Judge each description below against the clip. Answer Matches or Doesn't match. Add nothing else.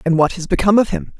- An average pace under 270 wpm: Doesn't match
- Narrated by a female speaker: Matches